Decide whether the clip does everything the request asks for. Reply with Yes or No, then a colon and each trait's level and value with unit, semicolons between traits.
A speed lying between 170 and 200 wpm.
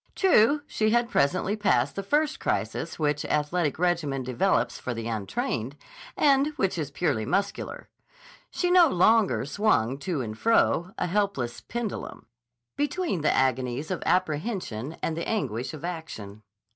No: average, 145 wpm